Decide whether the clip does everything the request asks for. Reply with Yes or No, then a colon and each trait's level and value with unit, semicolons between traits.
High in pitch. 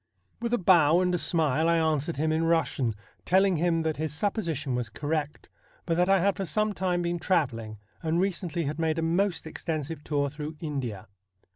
No: medium, 160 Hz